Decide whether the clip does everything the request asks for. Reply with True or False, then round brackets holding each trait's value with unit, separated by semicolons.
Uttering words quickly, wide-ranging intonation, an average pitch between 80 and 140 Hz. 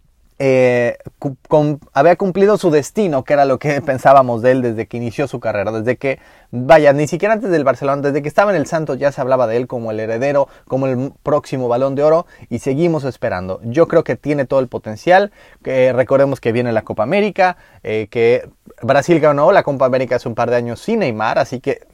False (220 wpm; 3.8 semitones; 135 Hz)